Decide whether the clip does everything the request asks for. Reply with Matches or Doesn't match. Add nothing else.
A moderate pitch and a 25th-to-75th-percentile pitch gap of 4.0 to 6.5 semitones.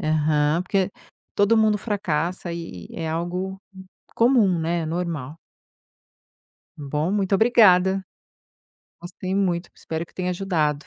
Doesn't match